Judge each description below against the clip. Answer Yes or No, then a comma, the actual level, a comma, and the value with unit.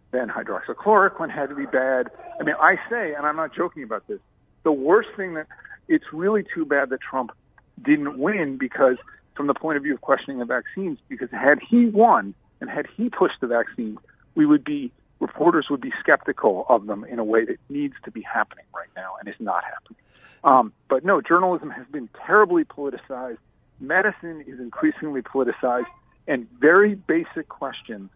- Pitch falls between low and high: Yes, medium, 165 Hz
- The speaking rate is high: No, average, 185 wpm